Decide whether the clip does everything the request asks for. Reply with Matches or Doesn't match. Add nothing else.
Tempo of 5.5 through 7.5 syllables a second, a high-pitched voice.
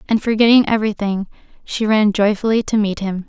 Matches